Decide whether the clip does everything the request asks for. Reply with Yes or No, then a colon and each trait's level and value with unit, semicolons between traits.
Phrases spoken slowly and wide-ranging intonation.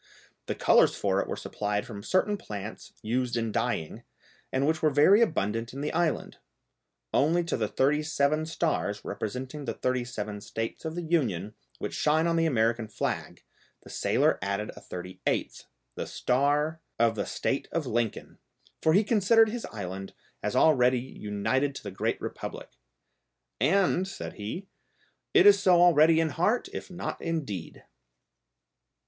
No: average, 160 wpm; wide, 7.0 semitones